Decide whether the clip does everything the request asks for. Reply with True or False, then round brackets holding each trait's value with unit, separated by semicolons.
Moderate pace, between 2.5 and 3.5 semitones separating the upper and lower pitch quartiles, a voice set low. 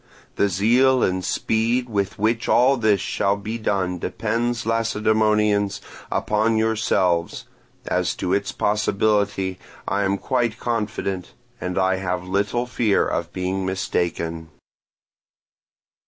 False (115 wpm; 3.0 semitones; 105 Hz)